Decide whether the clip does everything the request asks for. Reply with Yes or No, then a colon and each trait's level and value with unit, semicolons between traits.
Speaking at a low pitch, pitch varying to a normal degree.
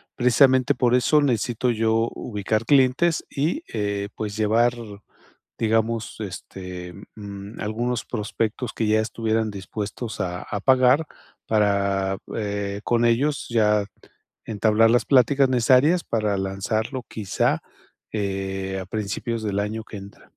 Yes: low, 110 Hz; average, 3.1 semitones